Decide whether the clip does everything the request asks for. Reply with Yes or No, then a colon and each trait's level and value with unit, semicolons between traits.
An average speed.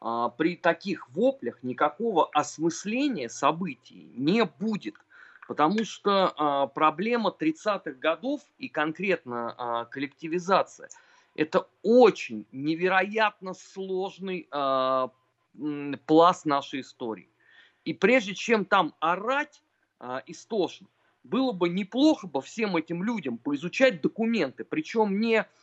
No: slow, 95 wpm